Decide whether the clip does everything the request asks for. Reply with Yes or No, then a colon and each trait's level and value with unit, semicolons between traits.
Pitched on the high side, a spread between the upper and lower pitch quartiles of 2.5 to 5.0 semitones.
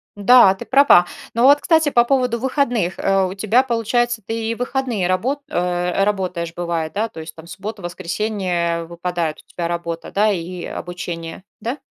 No: high, 195 Hz; wide, 5.4 semitones